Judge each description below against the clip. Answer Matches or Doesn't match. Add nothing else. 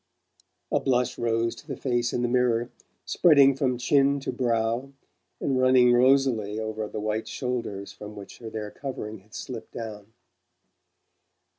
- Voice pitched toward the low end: Matches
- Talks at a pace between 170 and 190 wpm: Doesn't match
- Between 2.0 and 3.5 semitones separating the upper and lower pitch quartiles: Matches